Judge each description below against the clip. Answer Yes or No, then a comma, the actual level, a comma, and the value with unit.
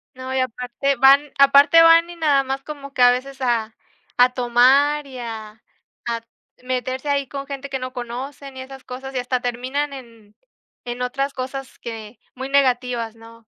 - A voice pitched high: Yes, very high, 260 Hz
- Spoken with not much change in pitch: Yes, narrow, 2.2 semitones